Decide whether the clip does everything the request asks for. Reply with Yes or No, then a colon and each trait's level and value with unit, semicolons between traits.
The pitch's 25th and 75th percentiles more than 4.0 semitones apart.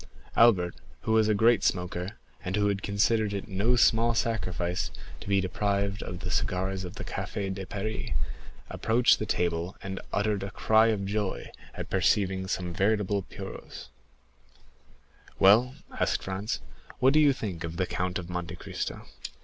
No: average, 2.8 semitones